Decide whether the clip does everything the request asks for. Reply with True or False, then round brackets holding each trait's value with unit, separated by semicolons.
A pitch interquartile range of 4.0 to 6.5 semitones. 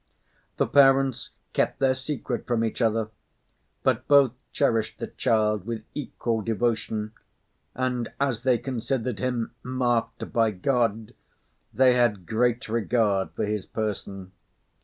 False (2.9 semitones)